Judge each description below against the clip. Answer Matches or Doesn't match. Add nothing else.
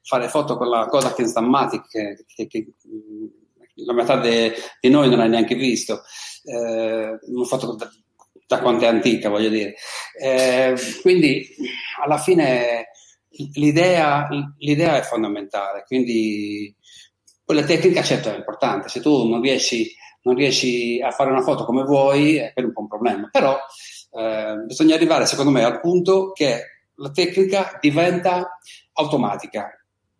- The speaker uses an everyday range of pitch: Doesn't match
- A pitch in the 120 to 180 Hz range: Matches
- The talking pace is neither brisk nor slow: Matches